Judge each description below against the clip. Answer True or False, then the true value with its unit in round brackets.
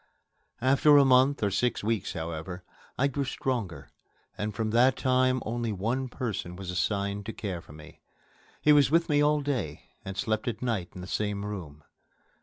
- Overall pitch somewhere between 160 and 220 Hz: False (110 Hz)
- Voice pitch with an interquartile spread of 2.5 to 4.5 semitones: False (5.3 semitones)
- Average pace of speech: True (180 wpm)